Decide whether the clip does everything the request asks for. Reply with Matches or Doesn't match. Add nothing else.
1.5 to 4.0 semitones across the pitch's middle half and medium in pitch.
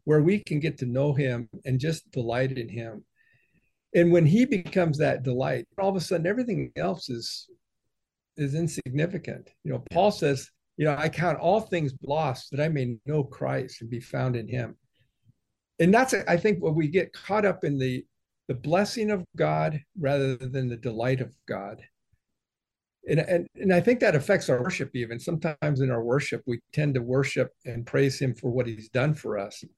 Doesn't match